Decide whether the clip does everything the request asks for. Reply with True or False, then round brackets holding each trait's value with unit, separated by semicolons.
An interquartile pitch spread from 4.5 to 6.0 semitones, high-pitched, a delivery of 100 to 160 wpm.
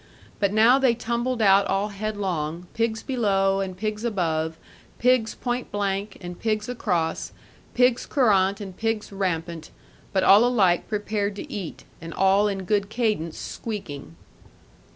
False (3.0 semitones; 205 Hz; 140 wpm)